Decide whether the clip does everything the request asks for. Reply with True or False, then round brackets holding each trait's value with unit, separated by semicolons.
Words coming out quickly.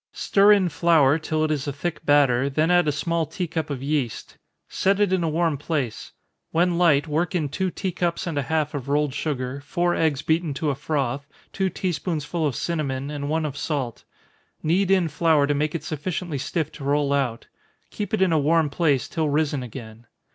True (210 wpm)